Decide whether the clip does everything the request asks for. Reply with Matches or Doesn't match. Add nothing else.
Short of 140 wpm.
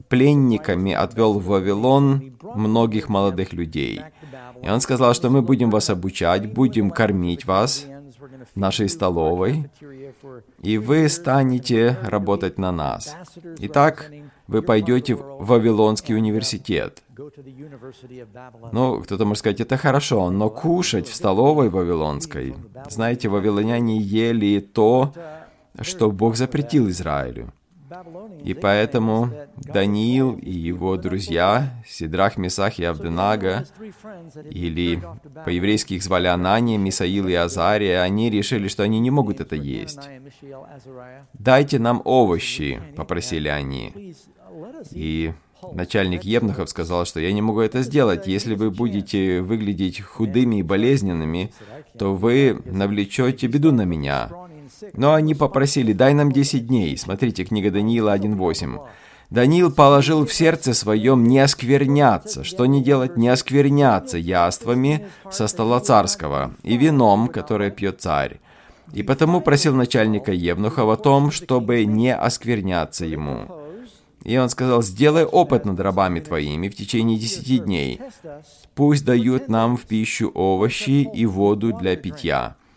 Matches